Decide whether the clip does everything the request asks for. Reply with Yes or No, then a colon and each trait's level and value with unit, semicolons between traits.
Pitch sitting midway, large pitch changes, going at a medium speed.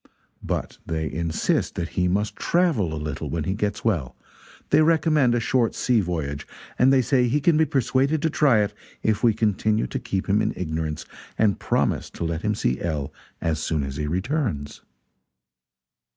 No: low, 105 Hz; wide, 8.0 semitones; average, 180 wpm